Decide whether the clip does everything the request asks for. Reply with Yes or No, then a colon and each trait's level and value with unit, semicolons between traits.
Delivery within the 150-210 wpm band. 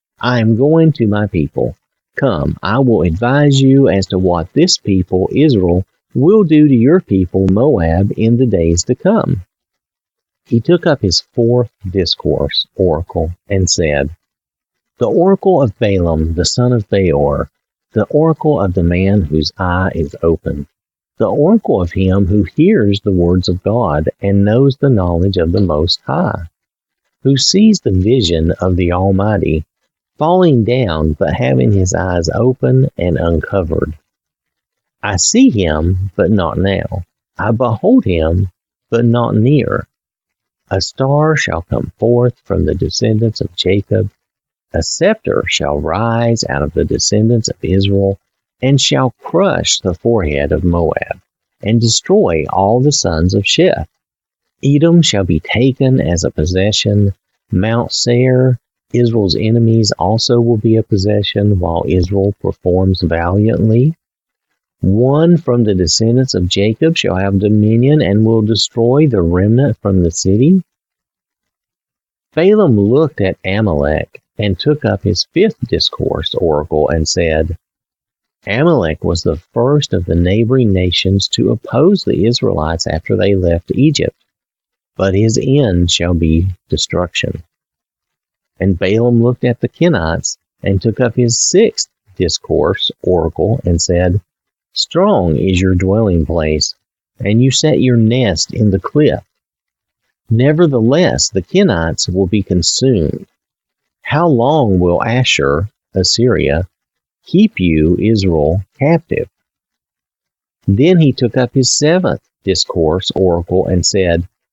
No: slow, 135 wpm